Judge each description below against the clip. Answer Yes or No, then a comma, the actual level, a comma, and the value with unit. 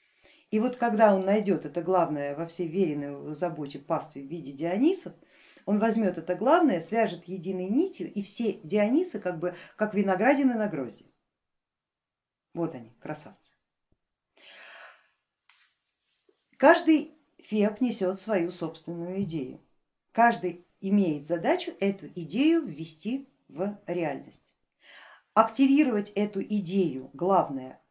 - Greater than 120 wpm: No, slow, 110 wpm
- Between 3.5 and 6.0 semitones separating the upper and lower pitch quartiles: Yes, average, 5.2 semitones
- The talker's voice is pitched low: No, high, 195 Hz